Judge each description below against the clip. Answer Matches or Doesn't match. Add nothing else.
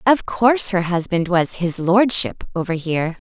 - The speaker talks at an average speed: Matches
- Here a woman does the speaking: Matches